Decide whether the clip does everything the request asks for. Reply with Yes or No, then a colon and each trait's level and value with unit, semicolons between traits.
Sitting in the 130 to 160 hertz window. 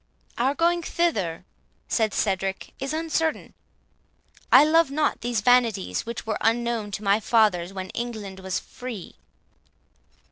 No: high, 230 Hz